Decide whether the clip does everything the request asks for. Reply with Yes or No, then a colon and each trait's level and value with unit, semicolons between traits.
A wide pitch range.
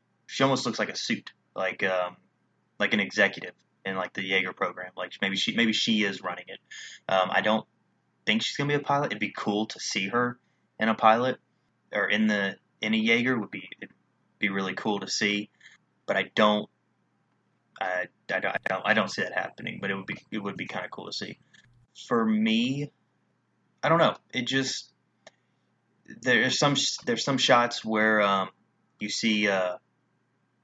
No: average, 4.4 semitones